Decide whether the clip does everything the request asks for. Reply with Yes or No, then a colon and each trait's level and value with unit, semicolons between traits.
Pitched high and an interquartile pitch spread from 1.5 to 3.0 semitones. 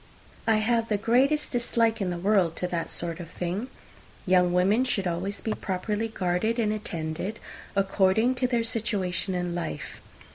No: high, 200 Hz; average, 4.1 semitones